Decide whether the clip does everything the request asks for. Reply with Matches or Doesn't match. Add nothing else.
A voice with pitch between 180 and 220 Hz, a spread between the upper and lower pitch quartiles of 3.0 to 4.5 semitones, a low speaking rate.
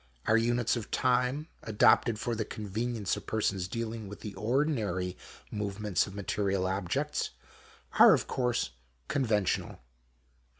Doesn't match